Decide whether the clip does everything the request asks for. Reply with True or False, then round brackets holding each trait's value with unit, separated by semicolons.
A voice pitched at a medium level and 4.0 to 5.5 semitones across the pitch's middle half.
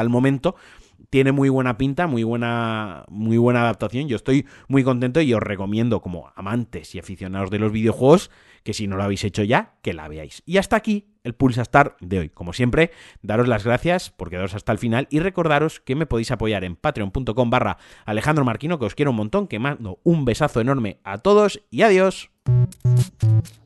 False (120 Hz; 4.7 semitones)